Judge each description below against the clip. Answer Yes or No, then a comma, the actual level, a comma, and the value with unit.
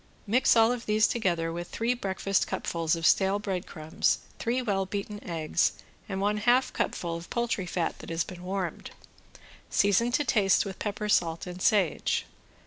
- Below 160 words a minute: No, average, 165 wpm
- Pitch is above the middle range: Yes, high, 195 Hz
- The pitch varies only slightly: No, average, 3.8 semitones